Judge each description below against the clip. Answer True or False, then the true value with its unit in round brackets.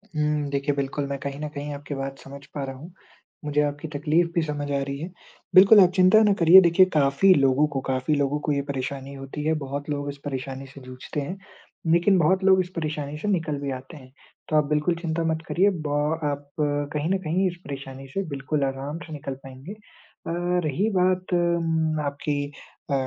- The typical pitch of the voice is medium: True (145 Hz)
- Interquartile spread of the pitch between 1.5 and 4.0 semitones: True (3.3 semitones)